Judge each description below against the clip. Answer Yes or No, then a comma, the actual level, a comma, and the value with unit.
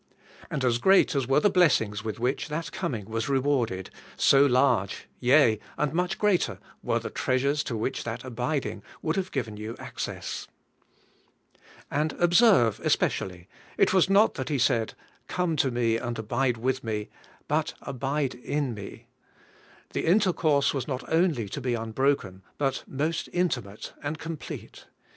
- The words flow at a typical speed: Yes, average, 155 wpm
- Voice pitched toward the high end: No, low, 135 Hz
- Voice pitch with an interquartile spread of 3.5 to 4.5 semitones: No, average, 5.0 semitones